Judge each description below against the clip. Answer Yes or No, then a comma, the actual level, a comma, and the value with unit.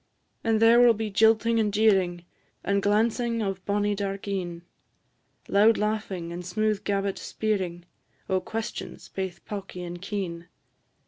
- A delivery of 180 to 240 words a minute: No, slow, 135 wpm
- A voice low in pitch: No, high, 200 Hz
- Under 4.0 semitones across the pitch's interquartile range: Yes, average, 2.7 semitones